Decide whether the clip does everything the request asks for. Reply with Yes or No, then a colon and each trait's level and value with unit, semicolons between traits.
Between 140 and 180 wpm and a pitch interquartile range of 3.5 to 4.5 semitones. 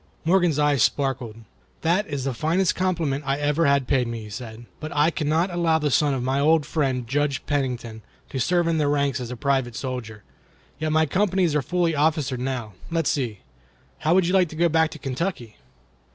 No: average, 200 wpm; average, 4.0 semitones